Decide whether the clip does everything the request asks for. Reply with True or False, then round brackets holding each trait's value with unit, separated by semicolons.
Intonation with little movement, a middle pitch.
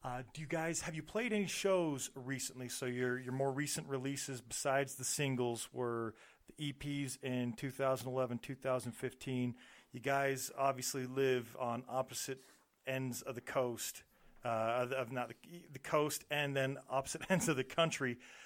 False (2.2 semitones; 130 Hz)